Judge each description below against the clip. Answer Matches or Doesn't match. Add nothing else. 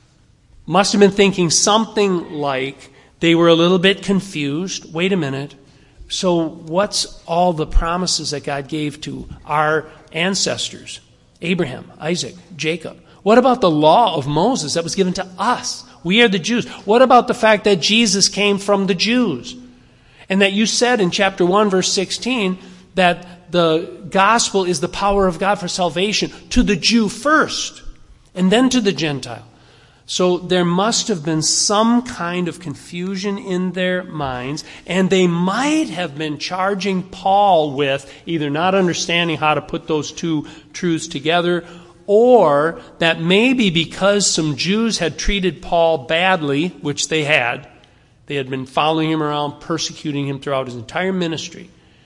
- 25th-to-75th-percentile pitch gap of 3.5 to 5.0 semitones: Matches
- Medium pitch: Matches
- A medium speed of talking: Matches